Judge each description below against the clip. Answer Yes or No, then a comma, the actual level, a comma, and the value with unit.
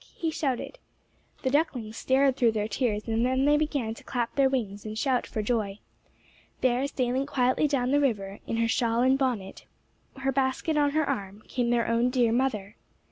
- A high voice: Yes, very high, 250 Hz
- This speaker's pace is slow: No, average, 190 wpm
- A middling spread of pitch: Yes, average, 3.2 semitones